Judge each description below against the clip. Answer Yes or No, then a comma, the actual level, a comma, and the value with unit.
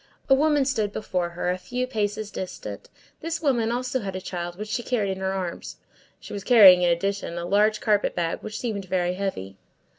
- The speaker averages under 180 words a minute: No, fast, 205 wpm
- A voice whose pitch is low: No, high, 200 Hz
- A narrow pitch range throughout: No, average, 4.1 semitones